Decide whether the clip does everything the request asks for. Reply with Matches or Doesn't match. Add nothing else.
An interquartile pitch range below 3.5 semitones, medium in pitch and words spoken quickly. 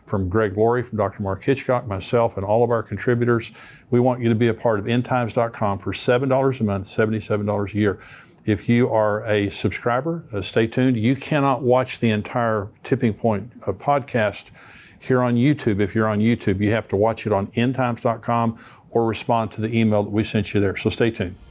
Doesn't match